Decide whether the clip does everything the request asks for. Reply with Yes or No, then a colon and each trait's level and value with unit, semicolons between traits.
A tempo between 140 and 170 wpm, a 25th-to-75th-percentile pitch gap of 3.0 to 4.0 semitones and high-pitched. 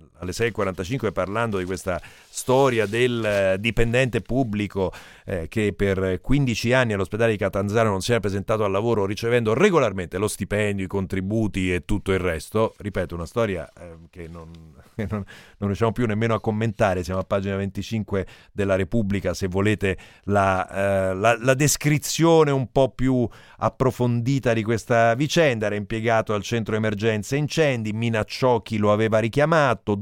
No: average, 160 wpm; average, 3.3 semitones; low, 105 Hz